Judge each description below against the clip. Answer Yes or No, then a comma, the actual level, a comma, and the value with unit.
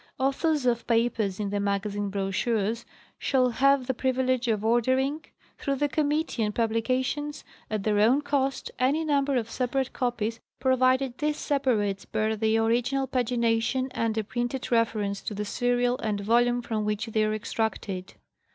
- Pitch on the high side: Yes, high, 240 Hz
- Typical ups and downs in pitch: Yes, average, 3.3 semitones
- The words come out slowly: No, average, 155 wpm